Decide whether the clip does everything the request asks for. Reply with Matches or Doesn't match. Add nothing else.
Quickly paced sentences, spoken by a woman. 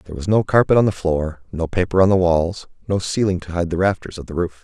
Doesn't match